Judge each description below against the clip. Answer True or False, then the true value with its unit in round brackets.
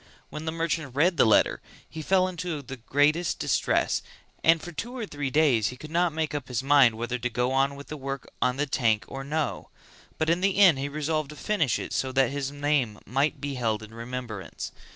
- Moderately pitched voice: True (145 Hz)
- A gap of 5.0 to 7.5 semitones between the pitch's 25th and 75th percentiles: False (3.9 semitones)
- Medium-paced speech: False (220 wpm)